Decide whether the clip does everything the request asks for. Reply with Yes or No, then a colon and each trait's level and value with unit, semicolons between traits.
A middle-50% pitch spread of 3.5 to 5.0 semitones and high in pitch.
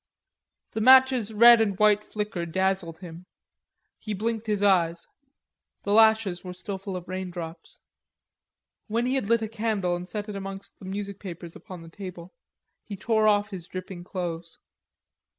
No: average, 3.1 semitones; high, 195 Hz